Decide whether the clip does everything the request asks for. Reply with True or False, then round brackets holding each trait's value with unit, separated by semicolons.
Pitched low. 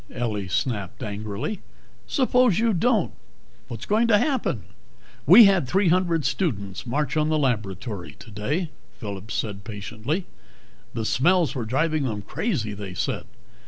True (130 Hz)